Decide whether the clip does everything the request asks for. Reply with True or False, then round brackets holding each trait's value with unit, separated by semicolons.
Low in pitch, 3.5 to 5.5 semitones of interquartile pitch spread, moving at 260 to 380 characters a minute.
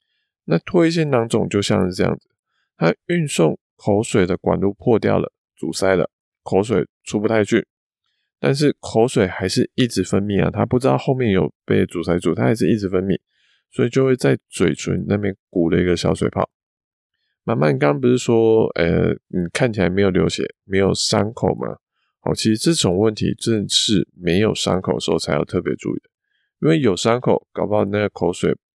True (105 Hz; 4.1 semitones; 280 characters per minute)